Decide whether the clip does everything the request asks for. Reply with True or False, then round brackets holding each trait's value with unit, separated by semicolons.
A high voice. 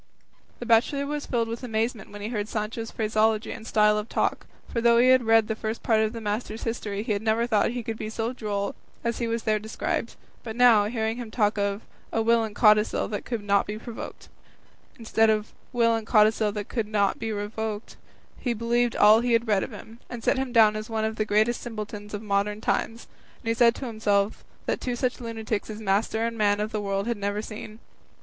True (220 Hz)